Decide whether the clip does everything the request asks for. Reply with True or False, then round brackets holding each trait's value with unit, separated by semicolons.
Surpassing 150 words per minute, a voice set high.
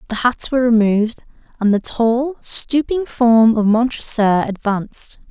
False (135 wpm; 230 Hz)